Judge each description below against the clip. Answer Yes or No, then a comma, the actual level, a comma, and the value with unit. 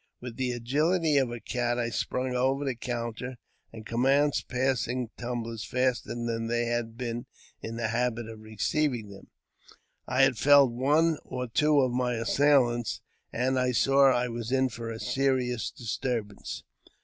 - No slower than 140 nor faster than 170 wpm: Yes, average, 160 wpm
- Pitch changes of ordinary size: No, narrow, 2.2 semitones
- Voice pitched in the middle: No, low, 125 Hz